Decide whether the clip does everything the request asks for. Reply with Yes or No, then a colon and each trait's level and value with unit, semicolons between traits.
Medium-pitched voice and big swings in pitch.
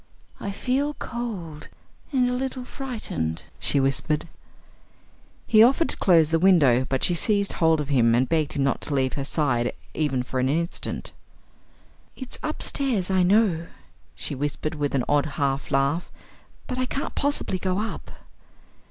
Yes: medium, 165 Hz; wide, 8.3 semitones